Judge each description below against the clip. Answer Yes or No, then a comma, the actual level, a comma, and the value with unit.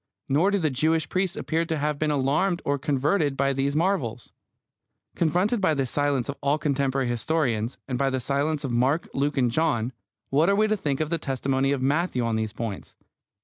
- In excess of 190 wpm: Yes, average, 200 wpm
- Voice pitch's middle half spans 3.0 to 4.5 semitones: Yes, average, 3.4 semitones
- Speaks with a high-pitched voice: No, medium, 140 Hz